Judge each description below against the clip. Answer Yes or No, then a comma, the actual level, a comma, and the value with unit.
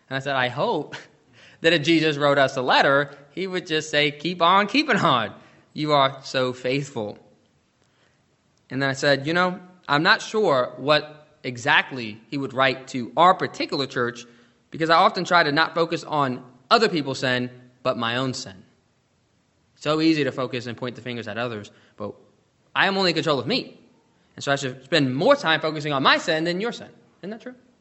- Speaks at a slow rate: No, average, 200 wpm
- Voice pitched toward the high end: No, medium, 140 Hz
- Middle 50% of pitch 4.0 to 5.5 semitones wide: Yes, average, 4.4 semitones